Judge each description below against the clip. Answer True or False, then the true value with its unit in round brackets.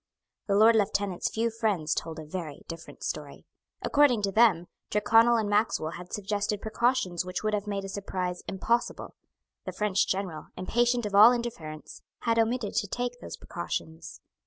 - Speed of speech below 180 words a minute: True (160 wpm)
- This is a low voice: False (205 Hz)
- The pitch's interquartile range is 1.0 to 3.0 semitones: False (4.0 semitones)